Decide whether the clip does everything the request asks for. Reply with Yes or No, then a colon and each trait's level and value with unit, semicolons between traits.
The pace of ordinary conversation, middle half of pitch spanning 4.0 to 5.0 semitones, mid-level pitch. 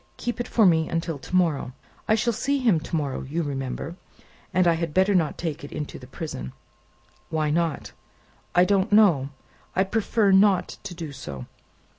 Yes: average, 180 wpm; average, 4.7 semitones; medium, 170 Hz